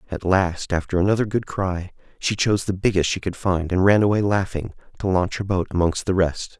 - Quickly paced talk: Yes, fast, 220 wpm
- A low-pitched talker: Yes, very low, 95 Hz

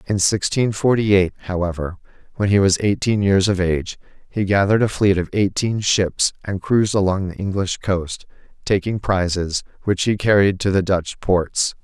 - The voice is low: Yes, very low, 95 Hz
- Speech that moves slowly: No, average, 170 wpm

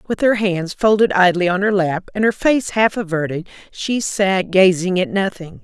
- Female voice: Yes, female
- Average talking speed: Yes, average, 190 wpm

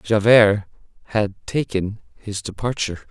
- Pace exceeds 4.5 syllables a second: No, 4.1 syllables/s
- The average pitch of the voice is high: No, low, 105 Hz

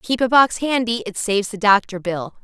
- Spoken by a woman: Yes, female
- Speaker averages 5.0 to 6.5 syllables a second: Yes, 5.3 syllables/s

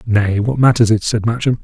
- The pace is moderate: No, fast, 220 wpm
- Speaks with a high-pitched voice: No, low, 115 Hz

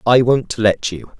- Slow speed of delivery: No, average, 200 wpm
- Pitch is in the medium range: No, low, 115 Hz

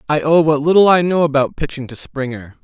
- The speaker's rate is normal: No, fast, 230 wpm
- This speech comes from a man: Yes, male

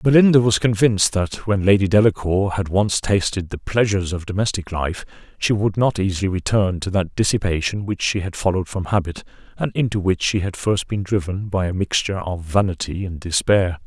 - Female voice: No, male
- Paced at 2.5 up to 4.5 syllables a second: No, 5.5 syllables/s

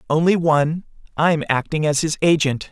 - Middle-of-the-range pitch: Yes, medium, 155 Hz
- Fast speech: No, average, 155 wpm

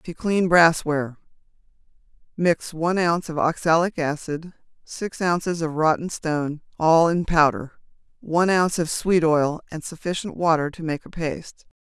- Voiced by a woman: Yes, female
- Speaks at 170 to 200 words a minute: No, average, 140 wpm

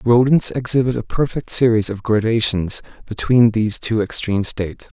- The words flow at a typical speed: Yes, average, 155 wpm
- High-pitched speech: No, low, 115 Hz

